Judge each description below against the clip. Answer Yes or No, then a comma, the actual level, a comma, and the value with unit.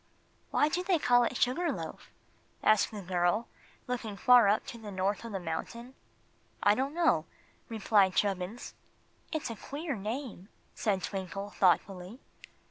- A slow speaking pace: No, average, 145 wpm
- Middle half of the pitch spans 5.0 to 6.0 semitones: No, average, 4.4 semitones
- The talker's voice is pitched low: No, high, 215 Hz